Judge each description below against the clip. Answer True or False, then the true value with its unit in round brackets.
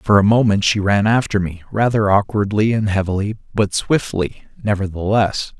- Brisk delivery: False (150 wpm)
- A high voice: False (105 Hz)